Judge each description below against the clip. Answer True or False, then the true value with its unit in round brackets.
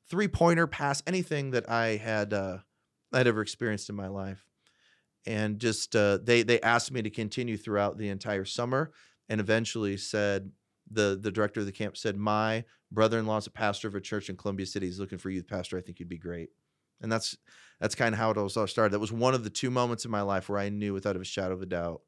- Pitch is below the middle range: True (105 Hz)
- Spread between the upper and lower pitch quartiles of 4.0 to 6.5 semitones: False (2.7 semitones)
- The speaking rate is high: True (235 wpm)